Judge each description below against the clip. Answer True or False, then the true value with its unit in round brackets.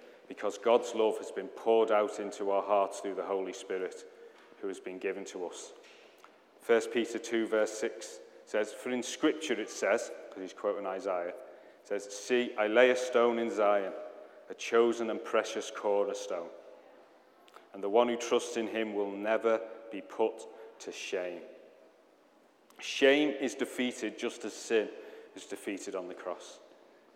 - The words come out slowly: False (165 wpm)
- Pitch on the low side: True (125 Hz)